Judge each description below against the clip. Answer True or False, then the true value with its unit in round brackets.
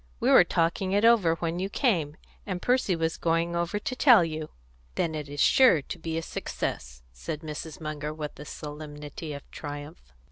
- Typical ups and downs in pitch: True (3.1 semitones)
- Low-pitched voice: False (160 Hz)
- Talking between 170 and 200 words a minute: True (185 wpm)